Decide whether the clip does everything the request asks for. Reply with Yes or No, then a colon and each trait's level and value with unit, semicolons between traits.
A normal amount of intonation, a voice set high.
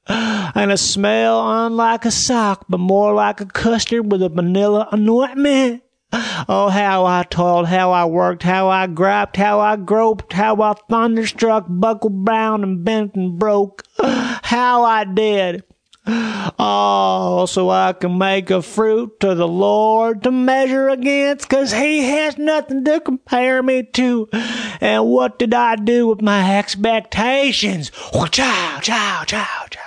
Yes: average, 3.9 semitones; high, 215 Hz